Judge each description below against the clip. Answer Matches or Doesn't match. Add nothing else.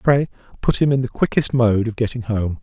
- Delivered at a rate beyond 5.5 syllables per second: Doesn't match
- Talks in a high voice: Doesn't match